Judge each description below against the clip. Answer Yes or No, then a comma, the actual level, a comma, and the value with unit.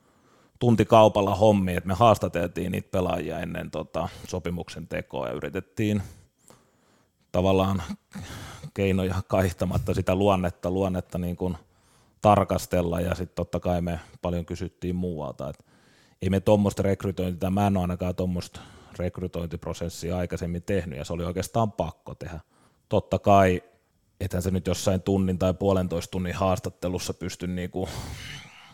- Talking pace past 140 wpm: No, average, 130 wpm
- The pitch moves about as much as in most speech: No, narrow, 2.0 semitones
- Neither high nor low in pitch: No, very low, 95 Hz